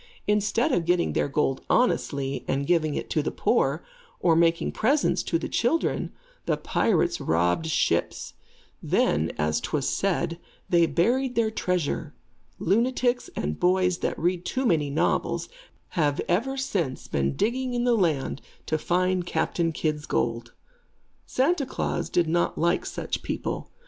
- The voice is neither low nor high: Yes, medium, 170 Hz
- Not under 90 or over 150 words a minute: Yes, average, 145 wpm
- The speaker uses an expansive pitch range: Yes, wide, 6.9 semitones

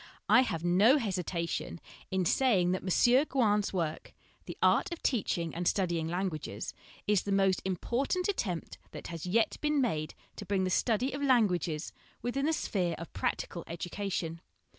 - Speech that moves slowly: No, average, 170 wpm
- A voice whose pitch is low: No, high, 190 Hz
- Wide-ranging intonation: Yes, wide, 5.9 semitones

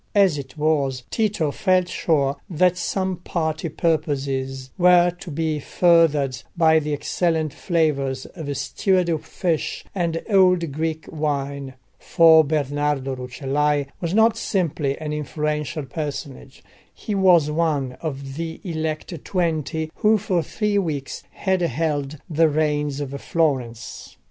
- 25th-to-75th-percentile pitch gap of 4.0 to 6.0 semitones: No, average, 3.4 semitones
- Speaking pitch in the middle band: Yes, medium, 155 Hz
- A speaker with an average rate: No, slow, 125 wpm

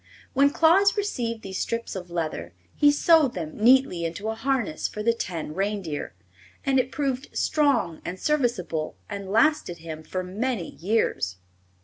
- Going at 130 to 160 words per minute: Yes, average, 150 wpm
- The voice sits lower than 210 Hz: No, high, 220 Hz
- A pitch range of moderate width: No, wide, 7.6 semitones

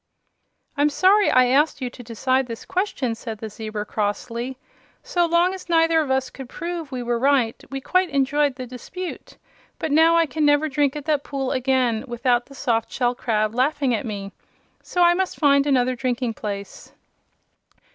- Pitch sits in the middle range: No, very high, 265 Hz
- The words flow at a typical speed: Yes, average, 180 wpm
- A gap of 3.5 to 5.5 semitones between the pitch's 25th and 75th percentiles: Yes, average, 4.4 semitones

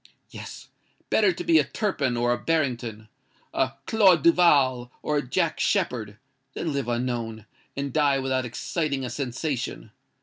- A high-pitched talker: No, low, 130 Hz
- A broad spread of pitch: No, average, 4.2 semitones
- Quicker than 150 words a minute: No, average, 140 wpm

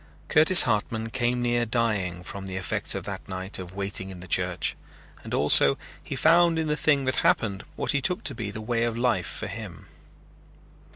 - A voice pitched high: No, low, 115 Hz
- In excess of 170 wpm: Yes, average, 195 wpm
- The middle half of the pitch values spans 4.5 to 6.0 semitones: Yes, average, 5.1 semitones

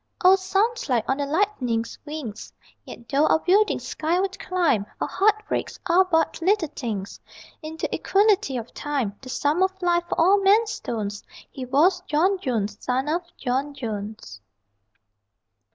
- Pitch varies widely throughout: Yes, wide, 7.3 semitones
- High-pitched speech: Yes, very high, 310 Hz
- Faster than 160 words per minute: No, average, 150 wpm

